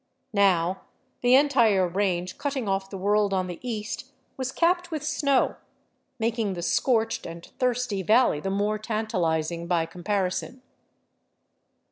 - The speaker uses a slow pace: Yes, slow, 130 wpm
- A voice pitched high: Yes, high, 210 Hz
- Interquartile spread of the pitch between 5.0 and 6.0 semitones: Yes, average, 5.3 semitones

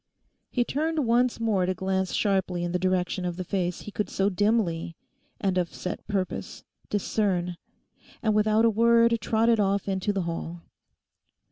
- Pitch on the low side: No, high, 195 Hz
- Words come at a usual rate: Yes, average, 150 wpm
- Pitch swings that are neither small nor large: Yes, average, 3.5 semitones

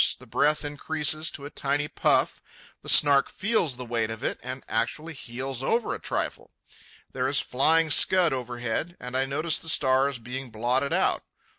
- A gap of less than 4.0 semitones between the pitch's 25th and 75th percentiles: Yes, average, 3.5 semitones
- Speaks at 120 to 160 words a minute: No, average, 170 wpm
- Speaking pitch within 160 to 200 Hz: No, low, 135 Hz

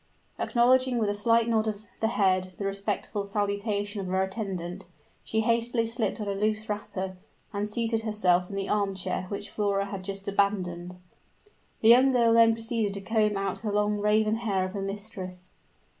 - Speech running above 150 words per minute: Yes, average, 180 wpm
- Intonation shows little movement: Yes, narrow, 2.3 semitones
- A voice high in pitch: Yes, high, 205 Hz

